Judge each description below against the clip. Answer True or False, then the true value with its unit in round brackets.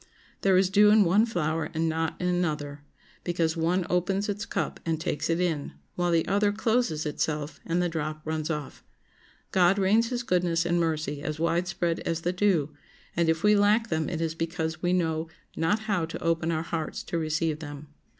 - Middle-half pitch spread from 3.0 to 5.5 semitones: False (2.6 semitones)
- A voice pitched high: False (165 Hz)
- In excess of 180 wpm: True (195 wpm)